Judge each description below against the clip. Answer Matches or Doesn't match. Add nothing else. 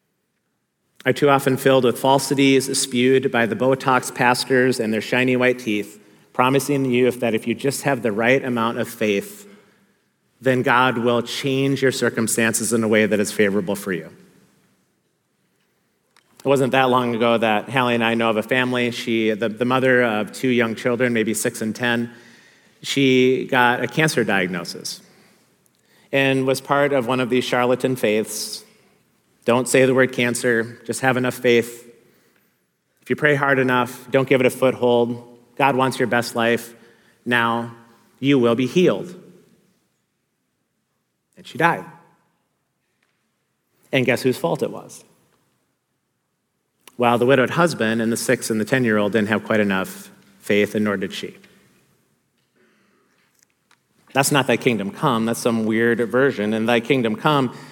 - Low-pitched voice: Matches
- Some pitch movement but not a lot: Doesn't match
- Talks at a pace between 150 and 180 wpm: Matches